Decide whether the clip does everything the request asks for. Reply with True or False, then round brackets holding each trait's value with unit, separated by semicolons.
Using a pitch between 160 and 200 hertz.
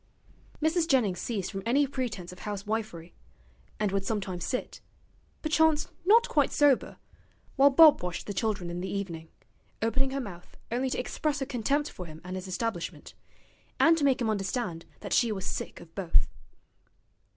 False (220 Hz)